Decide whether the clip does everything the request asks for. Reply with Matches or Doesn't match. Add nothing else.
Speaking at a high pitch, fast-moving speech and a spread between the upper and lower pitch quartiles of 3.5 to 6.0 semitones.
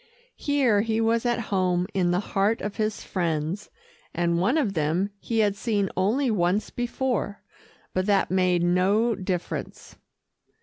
Doesn't match